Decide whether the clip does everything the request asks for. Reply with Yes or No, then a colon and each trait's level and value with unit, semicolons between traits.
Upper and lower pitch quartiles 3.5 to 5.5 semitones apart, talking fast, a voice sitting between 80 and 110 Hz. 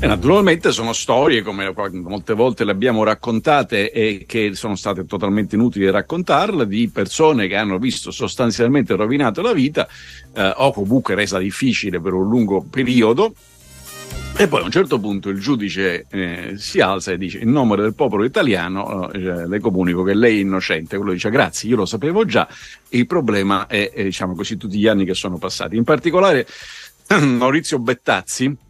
Yes: average, 4.2 semitones; fast, 175 wpm; low, 105 Hz